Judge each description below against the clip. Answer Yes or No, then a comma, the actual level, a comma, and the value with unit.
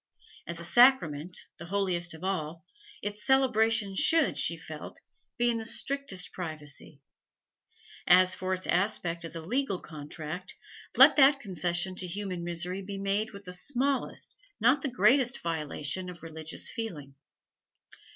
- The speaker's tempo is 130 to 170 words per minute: Yes, average, 140 wpm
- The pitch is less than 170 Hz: No, medium, 185 Hz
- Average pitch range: Yes, average, 5.0 semitones